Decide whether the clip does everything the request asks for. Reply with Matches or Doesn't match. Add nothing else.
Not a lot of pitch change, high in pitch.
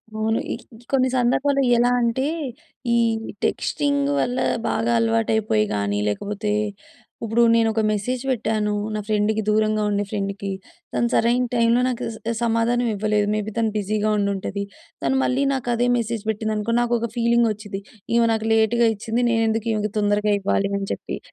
Matches